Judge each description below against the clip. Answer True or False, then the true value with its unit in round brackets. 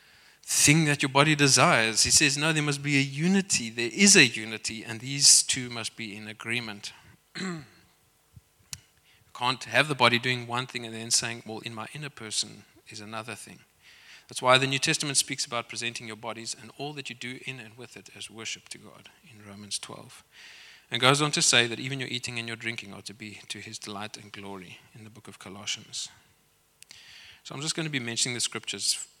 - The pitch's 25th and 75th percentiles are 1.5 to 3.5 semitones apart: False (4.1 semitones)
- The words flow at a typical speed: False (215 wpm)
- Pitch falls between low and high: False (120 Hz)